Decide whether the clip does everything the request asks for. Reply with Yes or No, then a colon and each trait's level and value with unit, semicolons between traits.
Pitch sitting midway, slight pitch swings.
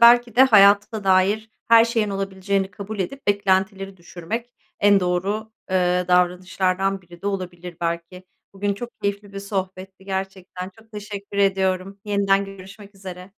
No: high, 195 Hz; narrow, 1.7 semitones